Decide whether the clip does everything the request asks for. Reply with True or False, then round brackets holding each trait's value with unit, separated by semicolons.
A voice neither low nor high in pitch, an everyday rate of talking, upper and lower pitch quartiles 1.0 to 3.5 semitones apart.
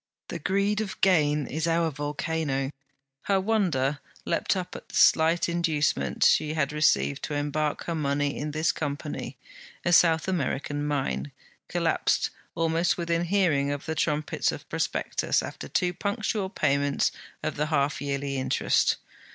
True (155 Hz; 145 wpm; 3.1 semitones)